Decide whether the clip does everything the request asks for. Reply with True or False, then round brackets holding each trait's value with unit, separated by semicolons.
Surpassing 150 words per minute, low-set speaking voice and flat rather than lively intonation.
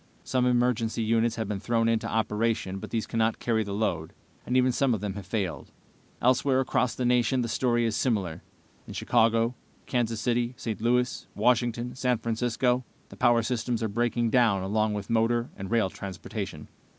True (175 wpm; 115 Hz; 2.0 semitones)